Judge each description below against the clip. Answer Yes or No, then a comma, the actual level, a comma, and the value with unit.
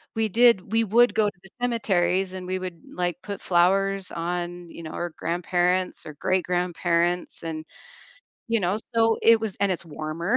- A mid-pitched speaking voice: Yes, medium, 180 Hz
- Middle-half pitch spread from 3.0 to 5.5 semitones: No, narrow, 2.6 semitones